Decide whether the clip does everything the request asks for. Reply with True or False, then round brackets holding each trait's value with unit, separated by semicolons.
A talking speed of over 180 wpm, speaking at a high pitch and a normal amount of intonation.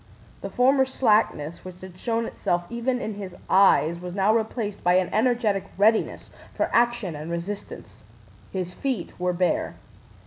False (150 wpm; 200 Hz; 4.4 semitones)